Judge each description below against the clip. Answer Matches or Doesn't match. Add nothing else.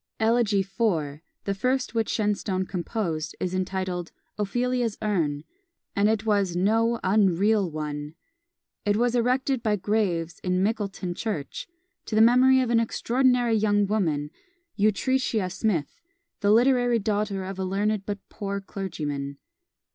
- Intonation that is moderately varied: Matches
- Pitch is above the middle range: Matches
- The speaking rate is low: Matches